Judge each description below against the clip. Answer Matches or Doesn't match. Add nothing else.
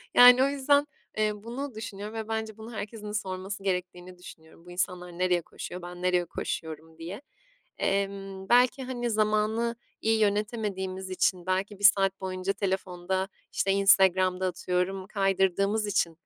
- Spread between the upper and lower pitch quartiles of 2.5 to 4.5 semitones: Matches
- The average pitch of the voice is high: Matches